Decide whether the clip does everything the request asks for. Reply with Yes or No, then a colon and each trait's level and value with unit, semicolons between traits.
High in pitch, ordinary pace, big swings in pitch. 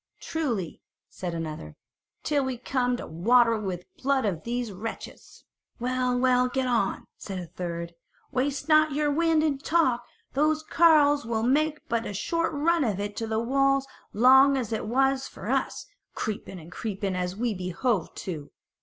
Yes: high, 245 Hz; average, 170 wpm; wide, 5.7 semitones